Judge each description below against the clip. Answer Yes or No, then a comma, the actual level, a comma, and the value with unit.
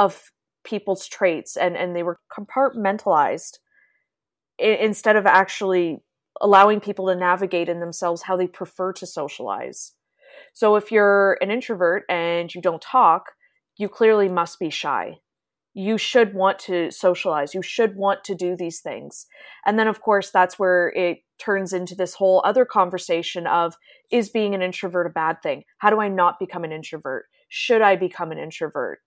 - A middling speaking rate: Yes, average, 165 wpm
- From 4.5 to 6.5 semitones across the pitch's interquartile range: No, average, 3.0 semitones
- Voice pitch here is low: No, high, 190 Hz